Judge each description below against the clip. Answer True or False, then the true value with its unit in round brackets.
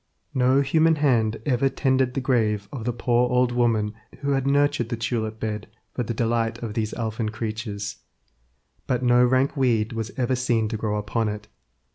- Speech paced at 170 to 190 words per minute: True (180 wpm)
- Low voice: True (120 Hz)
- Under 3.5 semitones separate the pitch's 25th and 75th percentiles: True (2.8 semitones)